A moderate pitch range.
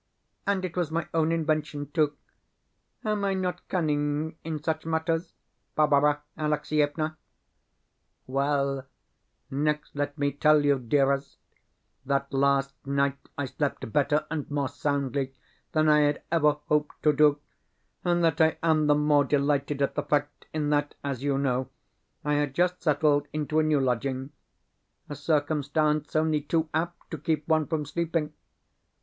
No: narrow, 1.8 semitones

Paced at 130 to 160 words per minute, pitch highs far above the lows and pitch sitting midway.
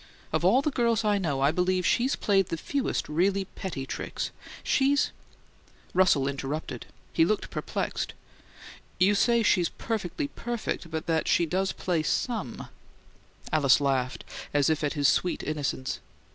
Yes: average, 155 wpm; wide, 5.9 semitones; medium, 180 Hz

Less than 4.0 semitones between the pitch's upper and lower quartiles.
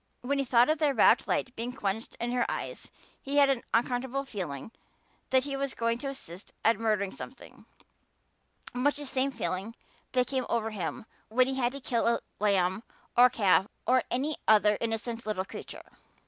Yes: average, 3.6 semitones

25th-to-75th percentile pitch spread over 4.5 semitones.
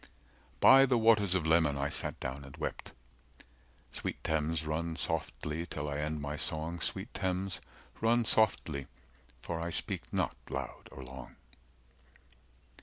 No: average, 4.0 semitones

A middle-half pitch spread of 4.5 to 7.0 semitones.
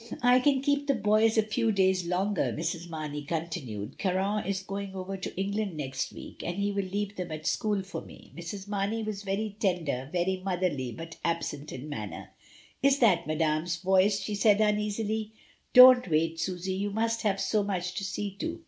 No: average, 3.7 semitones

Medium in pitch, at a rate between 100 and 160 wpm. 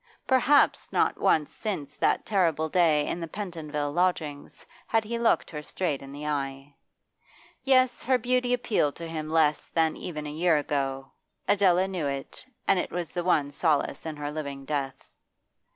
No: medium, 160 Hz; average, 170 wpm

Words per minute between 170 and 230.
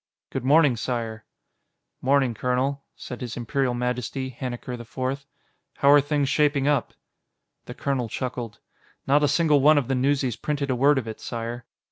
No: average, 160 wpm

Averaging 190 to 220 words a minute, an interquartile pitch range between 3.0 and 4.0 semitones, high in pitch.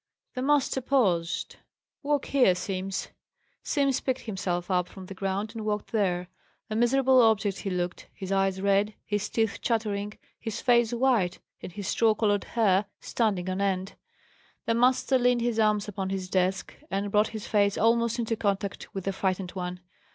No: average, 170 wpm; average, 3.4 semitones; high, 205 Hz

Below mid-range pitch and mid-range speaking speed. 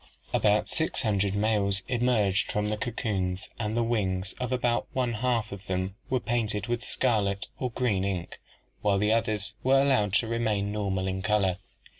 Yes: low, 105 Hz; average, 175 wpm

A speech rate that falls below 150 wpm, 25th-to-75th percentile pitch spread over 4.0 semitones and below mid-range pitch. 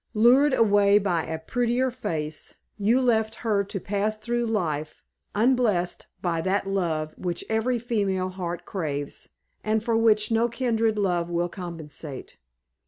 No: average, 140 wpm; average, 4.7 semitones; high, 205 Hz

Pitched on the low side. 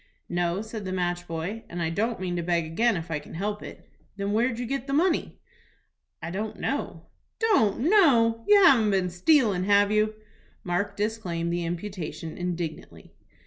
No: high, 200 Hz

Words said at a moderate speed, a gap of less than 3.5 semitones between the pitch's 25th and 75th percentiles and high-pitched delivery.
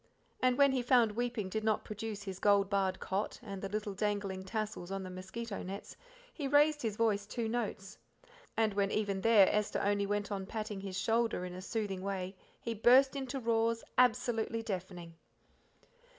Yes: average, 180 wpm; average, 2.9 semitones; high, 210 Hz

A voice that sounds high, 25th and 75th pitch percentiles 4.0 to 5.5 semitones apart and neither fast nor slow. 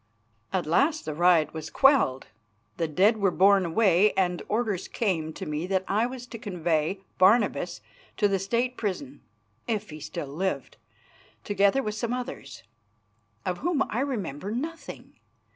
Yes: high, 200 Hz; average, 5.2 semitones; average, 150 wpm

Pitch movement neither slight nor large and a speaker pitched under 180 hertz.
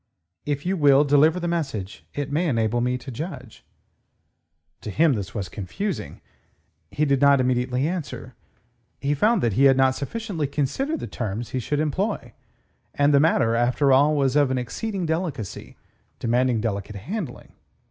Yes: average, 4.4 semitones; medium, 140 Hz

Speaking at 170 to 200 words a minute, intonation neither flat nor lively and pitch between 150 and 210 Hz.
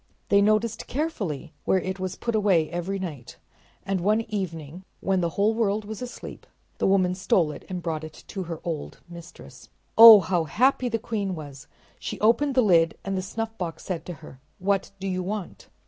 Yes: average, 190 wpm; average, 4.0 semitones; high, 190 Hz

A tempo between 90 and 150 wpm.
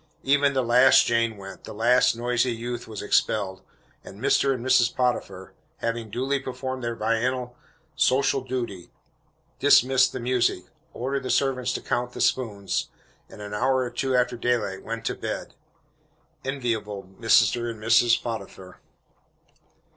Yes: average, 145 wpm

